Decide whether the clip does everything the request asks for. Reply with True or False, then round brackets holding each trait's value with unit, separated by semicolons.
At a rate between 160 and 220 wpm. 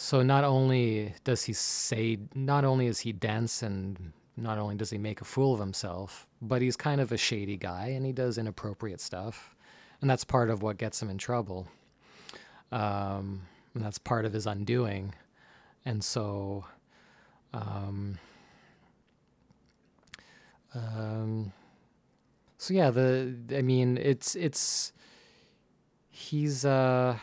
False (135 wpm)